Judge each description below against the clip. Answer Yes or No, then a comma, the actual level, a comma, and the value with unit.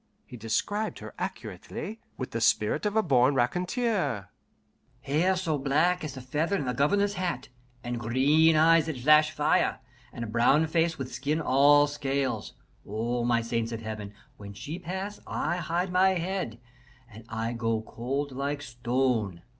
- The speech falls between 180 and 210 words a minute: No, average, 160 wpm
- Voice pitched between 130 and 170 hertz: Yes, medium, 140 Hz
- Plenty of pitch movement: Yes, wide, 6.0 semitones